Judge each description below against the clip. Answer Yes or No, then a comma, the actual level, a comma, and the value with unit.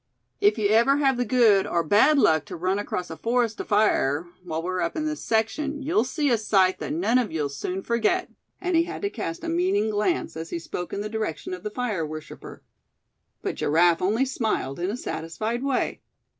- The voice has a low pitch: No, high, 215 Hz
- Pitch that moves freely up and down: Yes, wide, 6.7 semitones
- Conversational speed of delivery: No, fast, 210 wpm